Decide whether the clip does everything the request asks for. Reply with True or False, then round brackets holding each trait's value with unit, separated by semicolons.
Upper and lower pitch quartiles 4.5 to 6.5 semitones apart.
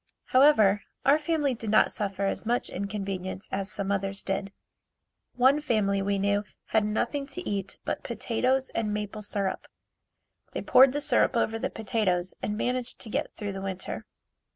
False (4.0 semitones)